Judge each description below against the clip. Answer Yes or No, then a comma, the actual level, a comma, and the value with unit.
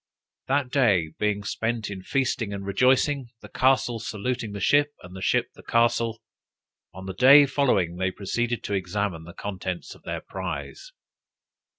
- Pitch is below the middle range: Yes, low, 110 Hz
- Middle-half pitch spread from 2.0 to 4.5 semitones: No, average, 4.9 semitones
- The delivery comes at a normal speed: Yes, average, 160 wpm